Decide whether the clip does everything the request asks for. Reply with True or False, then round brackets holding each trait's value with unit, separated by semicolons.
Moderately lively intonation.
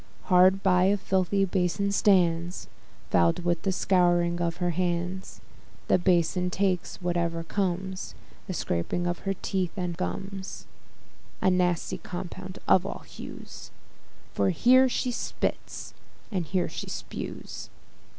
False (1.6 semitones)